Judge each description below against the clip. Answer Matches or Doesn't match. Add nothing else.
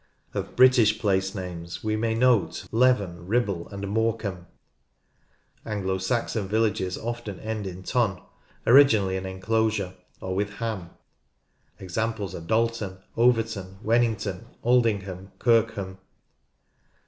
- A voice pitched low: Matches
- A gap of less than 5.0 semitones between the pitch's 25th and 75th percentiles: Matches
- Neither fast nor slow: Doesn't match